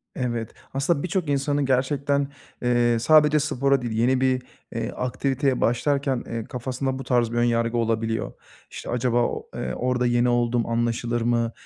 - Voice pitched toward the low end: Yes, low, 125 Hz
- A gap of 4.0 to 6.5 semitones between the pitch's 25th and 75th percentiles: No, narrow, 2.5 semitones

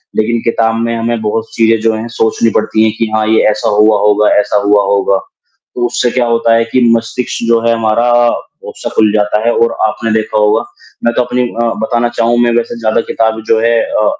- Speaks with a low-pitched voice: Yes, low, 115 Hz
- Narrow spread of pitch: Yes, narrow, 1.3 semitones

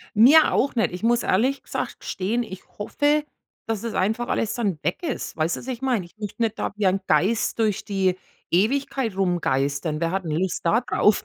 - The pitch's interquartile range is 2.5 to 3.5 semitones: No, average, 4.7 semitones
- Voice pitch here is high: Yes, high, 210 Hz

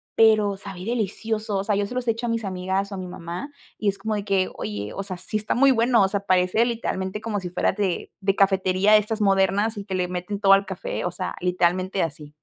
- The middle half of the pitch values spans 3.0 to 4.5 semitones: No, narrow, 2.5 semitones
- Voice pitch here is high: Yes, high, 195 Hz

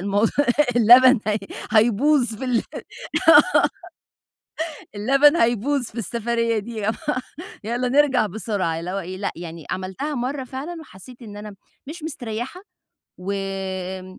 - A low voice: No, high, 225 Hz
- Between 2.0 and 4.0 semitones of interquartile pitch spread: No, average, 4.7 semitones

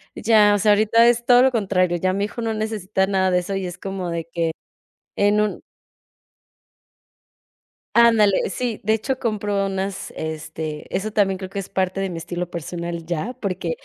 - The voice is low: No, high, 195 Hz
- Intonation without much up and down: No, average, 3.2 semitones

